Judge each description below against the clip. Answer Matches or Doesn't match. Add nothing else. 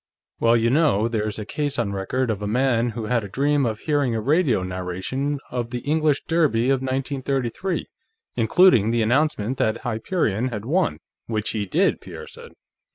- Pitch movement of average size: Matches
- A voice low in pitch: Matches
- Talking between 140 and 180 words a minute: Matches